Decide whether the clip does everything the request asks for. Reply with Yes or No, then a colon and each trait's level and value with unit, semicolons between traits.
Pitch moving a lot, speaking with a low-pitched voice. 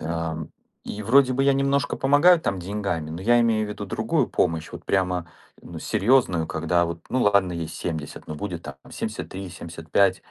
Yes: wide, 5.8 semitones; very low, 95 Hz